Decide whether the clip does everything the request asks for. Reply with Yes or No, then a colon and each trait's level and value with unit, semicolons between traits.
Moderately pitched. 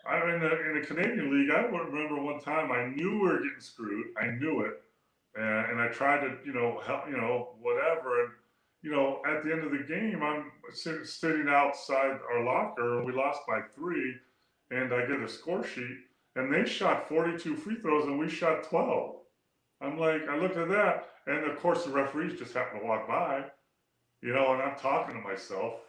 Yes: medium, 145 Hz